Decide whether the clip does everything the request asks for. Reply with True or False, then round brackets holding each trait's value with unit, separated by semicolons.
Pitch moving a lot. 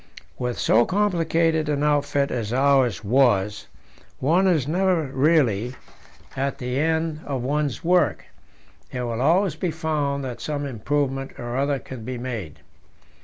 False (4.1 semitones)